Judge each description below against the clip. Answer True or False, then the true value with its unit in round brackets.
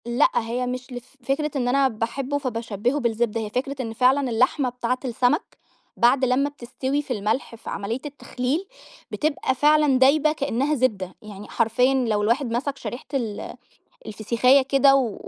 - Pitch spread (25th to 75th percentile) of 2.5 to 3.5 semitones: True (3.0 semitones)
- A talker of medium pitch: False (255 Hz)